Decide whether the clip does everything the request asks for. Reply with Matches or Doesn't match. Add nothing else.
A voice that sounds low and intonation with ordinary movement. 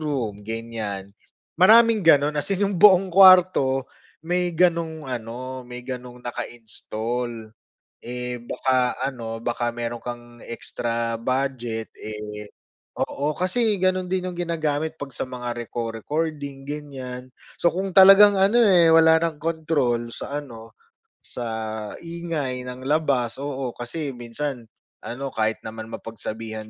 Doesn't match